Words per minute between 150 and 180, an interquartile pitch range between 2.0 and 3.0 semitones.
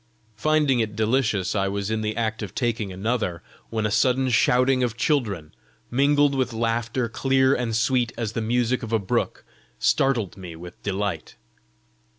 No: average, 165 wpm; average, 3.5 semitones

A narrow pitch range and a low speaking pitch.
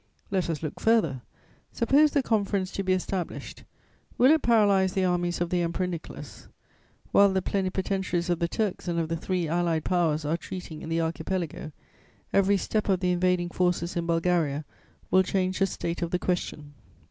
No: narrow, 2.3 semitones; medium, 180 Hz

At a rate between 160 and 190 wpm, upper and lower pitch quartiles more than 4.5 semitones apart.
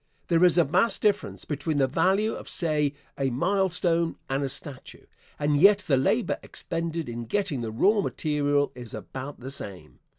Yes: average, 170 wpm; average, 5.0 semitones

